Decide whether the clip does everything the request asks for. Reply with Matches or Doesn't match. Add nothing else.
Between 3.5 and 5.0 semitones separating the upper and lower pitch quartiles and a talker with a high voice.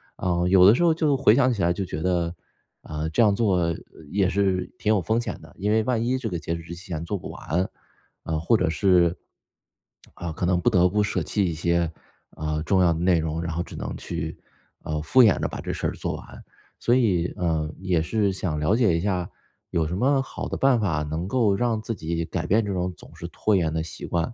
Doesn't match